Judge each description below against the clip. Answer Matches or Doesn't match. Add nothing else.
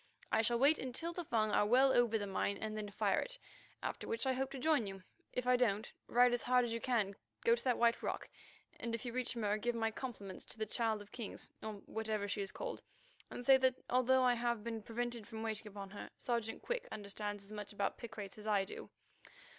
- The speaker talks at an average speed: Doesn't match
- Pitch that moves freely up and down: Doesn't match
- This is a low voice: Doesn't match